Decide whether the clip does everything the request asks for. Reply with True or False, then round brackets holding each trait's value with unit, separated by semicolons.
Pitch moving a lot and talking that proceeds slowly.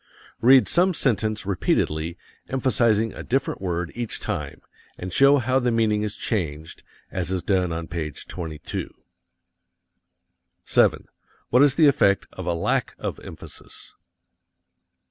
True (6.5 semitones; 130 wpm)